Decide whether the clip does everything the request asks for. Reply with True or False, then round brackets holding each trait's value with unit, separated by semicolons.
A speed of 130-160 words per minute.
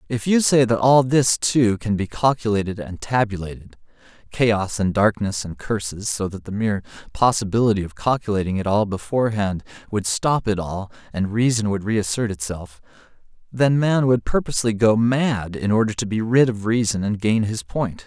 False (175 wpm)